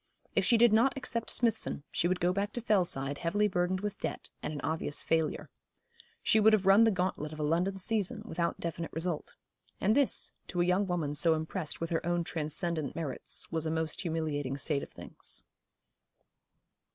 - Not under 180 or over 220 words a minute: Yes, average, 190 wpm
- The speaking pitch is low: No, medium, 175 Hz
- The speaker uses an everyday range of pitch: Yes, average, 4.3 semitones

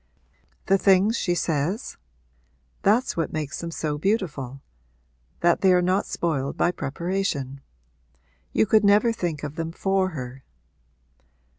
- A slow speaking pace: Yes, slow, 130 wpm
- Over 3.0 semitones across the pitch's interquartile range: Yes, average, 4.9 semitones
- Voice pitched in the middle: Yes, medium, 170 Hz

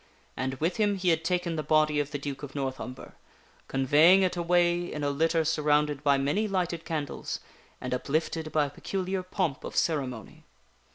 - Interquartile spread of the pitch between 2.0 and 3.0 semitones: No, average, 3.6 semitones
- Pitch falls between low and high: Yes, medium, 155 Hz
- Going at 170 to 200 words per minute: Yes, average, 180 wpm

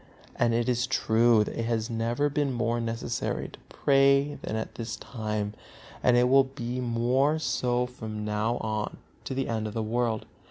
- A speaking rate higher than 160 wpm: Yes, average, 185 wpm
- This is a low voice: Yes, low, 120 Hz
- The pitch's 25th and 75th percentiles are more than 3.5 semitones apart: No, narrow, 2.4 semitones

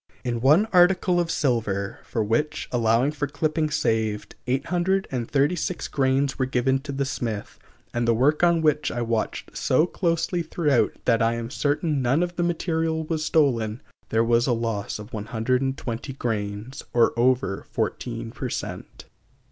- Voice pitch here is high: No, low, 130 Hz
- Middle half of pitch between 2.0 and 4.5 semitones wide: No, average, 5.0 semitones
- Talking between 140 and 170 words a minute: Yes, average, 155 wpm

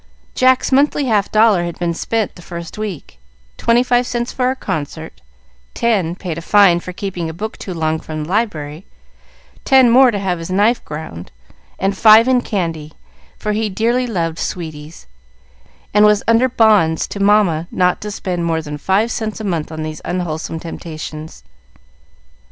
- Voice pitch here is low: No, high, 190 Hz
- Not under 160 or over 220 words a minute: Yes, average, 170 wpm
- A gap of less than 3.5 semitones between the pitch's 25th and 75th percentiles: No, wide, 5.4 semitones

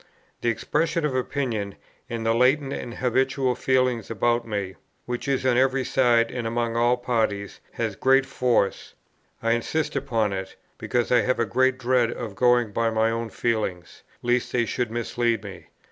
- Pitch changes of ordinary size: No, narrow, 2.2 semitones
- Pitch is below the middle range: Yes, low, 120 Hz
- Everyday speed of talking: Yes, average, 170 wpm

